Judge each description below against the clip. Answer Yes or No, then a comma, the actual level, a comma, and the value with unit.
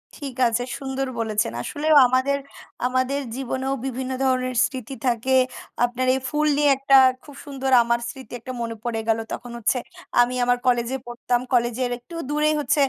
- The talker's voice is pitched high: Yes, very high, 255 Hz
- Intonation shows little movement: Yes, narrow, 2.1 semitones